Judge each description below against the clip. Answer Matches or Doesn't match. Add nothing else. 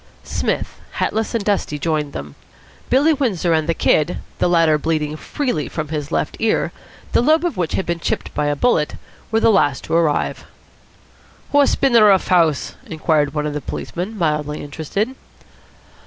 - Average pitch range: Doesn't match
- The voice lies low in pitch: Doesn't match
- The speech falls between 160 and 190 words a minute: Matches